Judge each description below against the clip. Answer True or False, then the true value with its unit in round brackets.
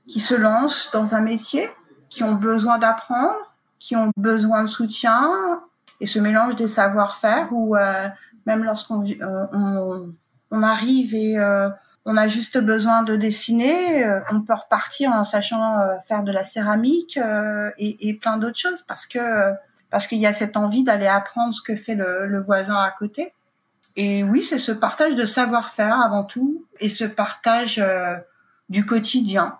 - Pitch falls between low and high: False (220 Hz)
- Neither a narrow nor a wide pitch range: False (2.3 semitones)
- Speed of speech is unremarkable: True (170 wpm)